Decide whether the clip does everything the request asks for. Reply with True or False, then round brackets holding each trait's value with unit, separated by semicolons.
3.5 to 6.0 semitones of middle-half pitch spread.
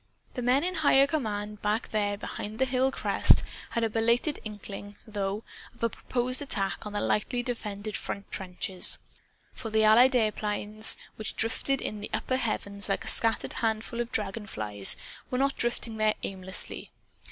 False (3.0 semitones)